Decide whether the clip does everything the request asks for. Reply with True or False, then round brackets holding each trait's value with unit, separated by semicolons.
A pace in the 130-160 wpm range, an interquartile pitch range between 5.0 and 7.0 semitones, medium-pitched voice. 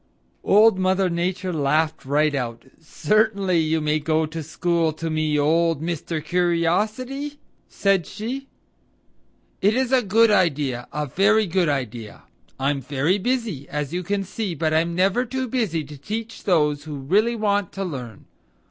True (155 wpm; 5.3 semitones; 170 Hz)